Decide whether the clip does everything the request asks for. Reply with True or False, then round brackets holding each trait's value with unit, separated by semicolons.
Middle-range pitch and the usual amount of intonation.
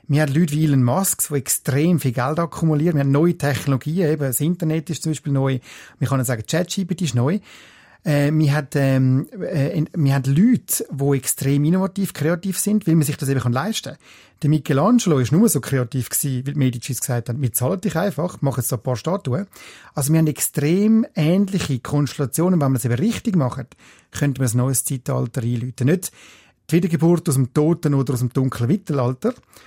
True (145 Hz; 4.4 semitones)